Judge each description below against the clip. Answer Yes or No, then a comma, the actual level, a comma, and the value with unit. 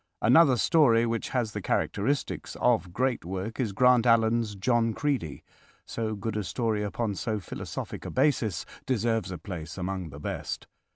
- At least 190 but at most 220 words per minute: No, average, 160 wpm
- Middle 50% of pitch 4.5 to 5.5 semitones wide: No, average, 3.7 semitones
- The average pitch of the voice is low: Yes, low, 110 Hz